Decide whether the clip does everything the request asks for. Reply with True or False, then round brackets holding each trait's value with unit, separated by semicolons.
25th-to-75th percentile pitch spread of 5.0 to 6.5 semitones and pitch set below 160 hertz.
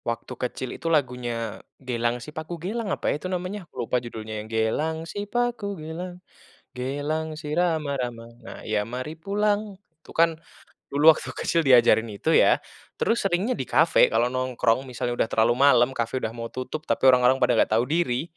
True (5.6 semitones; 135 Hz)